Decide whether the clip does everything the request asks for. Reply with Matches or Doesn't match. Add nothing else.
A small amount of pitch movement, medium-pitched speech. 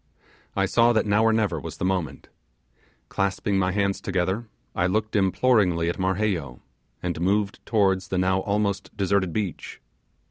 Doesn't match